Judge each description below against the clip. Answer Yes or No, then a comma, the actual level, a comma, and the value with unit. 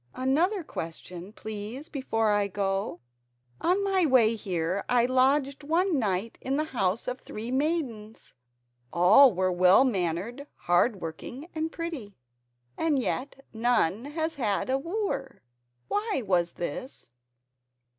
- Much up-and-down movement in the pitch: Yes, wide, 6.6 semitones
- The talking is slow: Yes, slow, 125 wpm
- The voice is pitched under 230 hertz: No, high, 245 Hz